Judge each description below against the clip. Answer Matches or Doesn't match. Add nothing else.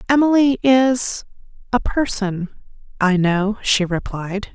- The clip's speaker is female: Matches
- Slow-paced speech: Matches